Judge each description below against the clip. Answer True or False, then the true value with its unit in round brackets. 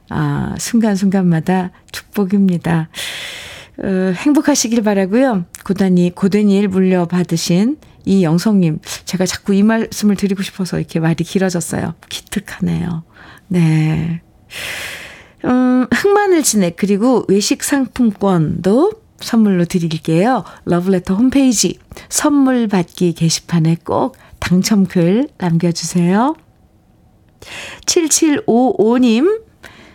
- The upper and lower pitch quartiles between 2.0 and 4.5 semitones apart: False (5.1 semitones)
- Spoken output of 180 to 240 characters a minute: True (235 characters per minute)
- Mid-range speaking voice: False (195 Hz)